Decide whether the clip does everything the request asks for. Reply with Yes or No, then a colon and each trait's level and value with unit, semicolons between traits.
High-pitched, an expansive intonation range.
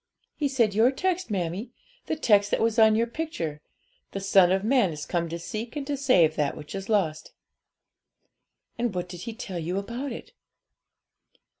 Yes: high, 210 Hz; wide, 5.8 semitones